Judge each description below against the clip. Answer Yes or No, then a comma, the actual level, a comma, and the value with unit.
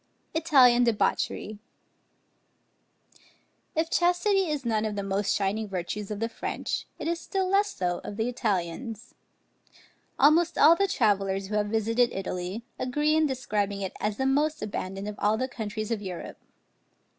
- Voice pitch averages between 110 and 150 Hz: No, high, 220 Hz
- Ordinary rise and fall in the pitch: No, wide, 6.5 semitones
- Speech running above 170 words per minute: No, average, 155 wpm